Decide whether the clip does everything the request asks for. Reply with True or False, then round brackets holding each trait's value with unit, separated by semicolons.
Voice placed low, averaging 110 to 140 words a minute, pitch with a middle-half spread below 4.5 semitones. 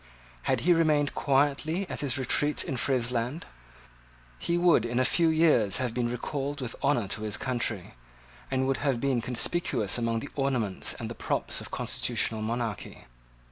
False (130 Hz; 165 wpm; 3.9 semitones)